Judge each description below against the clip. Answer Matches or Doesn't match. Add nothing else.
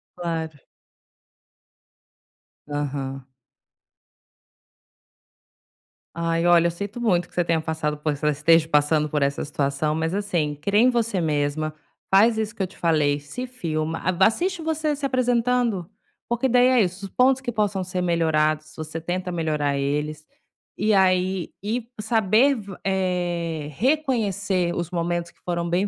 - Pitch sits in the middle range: Matches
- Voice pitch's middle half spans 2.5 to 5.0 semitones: Doesn't match